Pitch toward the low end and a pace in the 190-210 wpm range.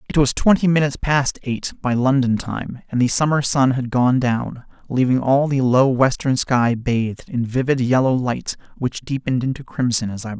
Yes: low, 130 Hz; average, 200 wpm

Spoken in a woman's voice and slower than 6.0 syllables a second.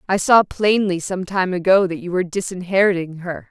Yes: female; 5.4 syllables/s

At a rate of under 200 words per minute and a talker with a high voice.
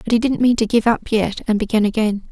No: fast, 285 wpm; high, 220 Hz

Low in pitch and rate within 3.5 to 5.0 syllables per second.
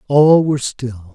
Yes: low, 130 Hz; 4.1 syllables/s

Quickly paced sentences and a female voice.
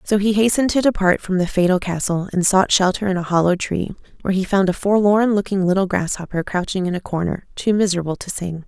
Yes: fast, 220 wpm; female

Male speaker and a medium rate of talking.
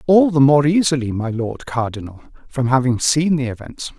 Yes: male; average, 180 wpm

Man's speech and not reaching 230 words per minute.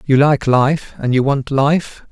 Yes: male; average, 200 wpm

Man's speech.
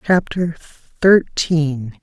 No: female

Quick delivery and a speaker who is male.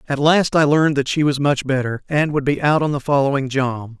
Yes: fast, 255 wpm; male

